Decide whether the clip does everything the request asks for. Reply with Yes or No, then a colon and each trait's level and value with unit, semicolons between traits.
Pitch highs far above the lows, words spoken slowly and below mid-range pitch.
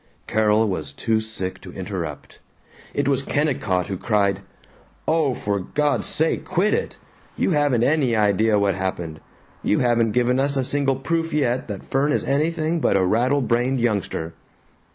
No: wide, 5.8 semitones; average, 160 wpm; low, 120 Hz